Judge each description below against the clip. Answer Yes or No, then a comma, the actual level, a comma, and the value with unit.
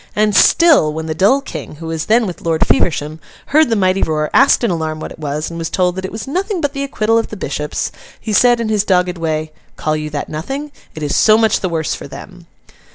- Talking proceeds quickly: Yes, fast, 245 wpm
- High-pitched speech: No, medium, 180 Hz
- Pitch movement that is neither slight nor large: No, wide, 6.3 semitones